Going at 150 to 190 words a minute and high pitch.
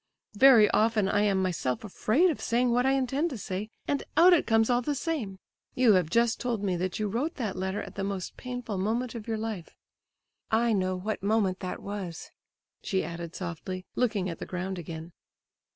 No: average, 200 wpm; high, 210 Hz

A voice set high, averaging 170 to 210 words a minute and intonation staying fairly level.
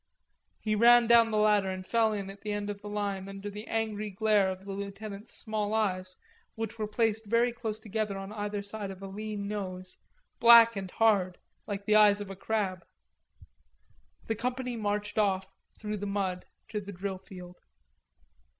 Yes: high, 205 Hz; average, 180 wpm; narrow, 2.0 semitones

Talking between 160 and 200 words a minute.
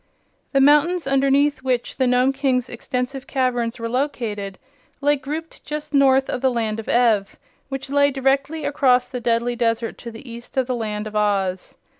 Yes: average, 175 wpm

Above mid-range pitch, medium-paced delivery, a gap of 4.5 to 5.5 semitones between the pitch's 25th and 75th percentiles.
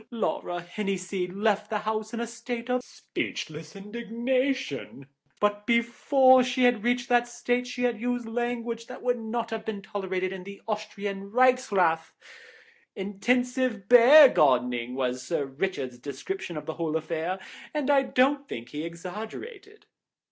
Yes: high, 220 Hz; average, 145 wpm; average, 5.1 semitones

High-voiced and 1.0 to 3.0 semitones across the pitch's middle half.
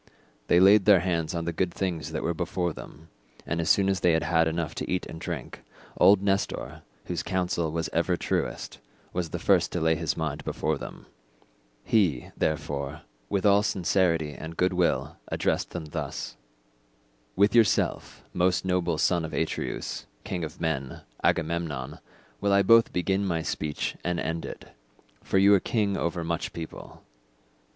No: very low, 85 Hz; average, 2.7 semitones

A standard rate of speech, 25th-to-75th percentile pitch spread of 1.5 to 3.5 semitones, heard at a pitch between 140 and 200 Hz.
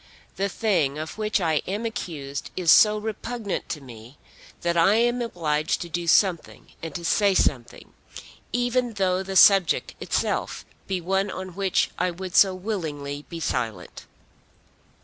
No: average, 150 wpm; average, 4.5 semitones; medium, 185 Hz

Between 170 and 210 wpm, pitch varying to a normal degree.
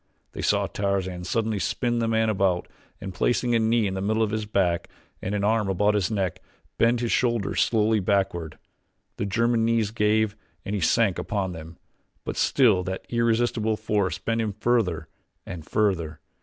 Yes: average, 175 wpm; average, 3.1 semitones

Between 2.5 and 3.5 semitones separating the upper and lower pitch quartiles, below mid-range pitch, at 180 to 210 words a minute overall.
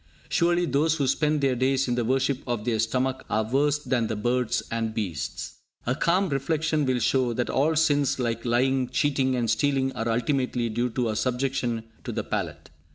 Yes: average, 2.9 semitones; low, 130 Hz; average, 190 wpm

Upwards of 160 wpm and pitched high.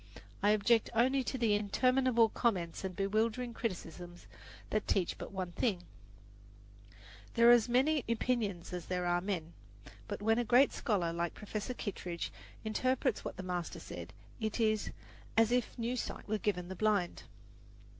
No: average, 155 wpm; high, 215 Hz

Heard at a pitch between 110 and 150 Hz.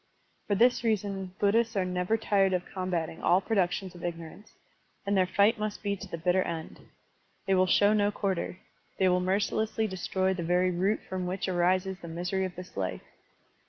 No: high, 190 Hz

